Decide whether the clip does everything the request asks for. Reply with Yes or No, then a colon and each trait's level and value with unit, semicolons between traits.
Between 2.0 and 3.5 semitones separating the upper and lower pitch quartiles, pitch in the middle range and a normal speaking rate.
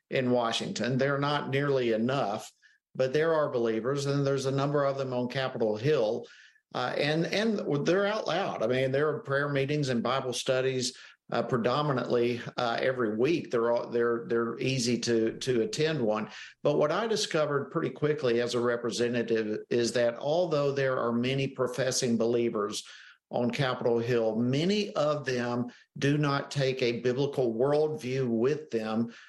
No: average, 3.1 semitones; low, 130 Hz; average, 160 wpm